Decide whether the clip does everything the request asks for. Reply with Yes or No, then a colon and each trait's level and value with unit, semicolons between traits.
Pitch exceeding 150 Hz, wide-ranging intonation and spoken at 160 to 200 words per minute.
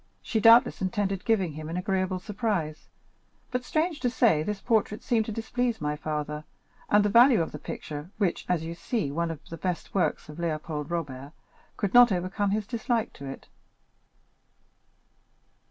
Yes: high, 190 Hz; wide, 6.0 semitones; average, 170 wpm